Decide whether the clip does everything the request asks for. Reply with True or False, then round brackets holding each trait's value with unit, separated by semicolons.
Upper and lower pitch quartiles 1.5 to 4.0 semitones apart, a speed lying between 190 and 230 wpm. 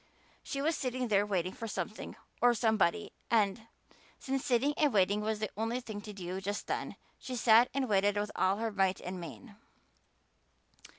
False (3.3 semitones; 175 wpm)